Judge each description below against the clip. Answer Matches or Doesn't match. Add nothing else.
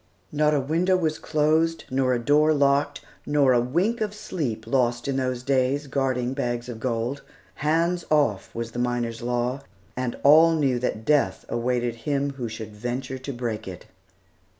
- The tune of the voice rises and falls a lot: Doesn't match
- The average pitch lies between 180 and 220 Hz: Doesn't match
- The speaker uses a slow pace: Doesn't match